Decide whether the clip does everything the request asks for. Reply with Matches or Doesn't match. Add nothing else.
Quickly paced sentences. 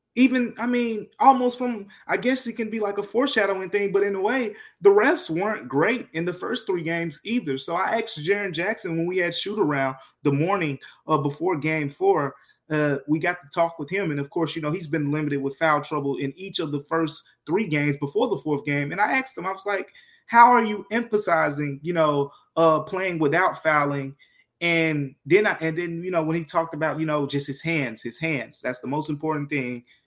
Matches